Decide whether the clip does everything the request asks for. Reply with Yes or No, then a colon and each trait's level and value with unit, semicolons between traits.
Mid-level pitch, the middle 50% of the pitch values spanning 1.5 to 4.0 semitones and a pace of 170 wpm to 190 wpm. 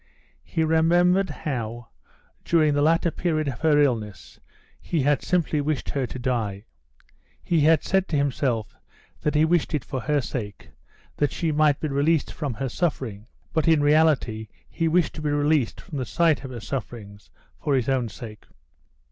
No: medium, 145 Hz; average, 4.4 semitones; average, 175 wpm